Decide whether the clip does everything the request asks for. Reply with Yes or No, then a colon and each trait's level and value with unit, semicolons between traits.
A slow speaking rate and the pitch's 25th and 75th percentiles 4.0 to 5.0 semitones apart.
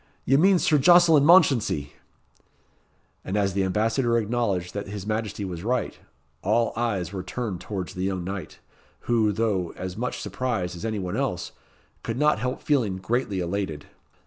No: average, 160 wpm; average, 4.6 semitones